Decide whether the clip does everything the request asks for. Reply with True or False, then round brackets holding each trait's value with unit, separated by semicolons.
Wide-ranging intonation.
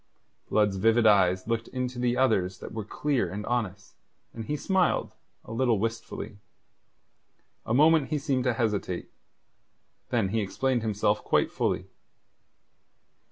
False (3.6 semitones)